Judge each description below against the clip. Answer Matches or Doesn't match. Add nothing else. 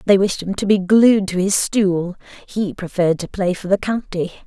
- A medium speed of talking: Doesn't match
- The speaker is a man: Doesn't match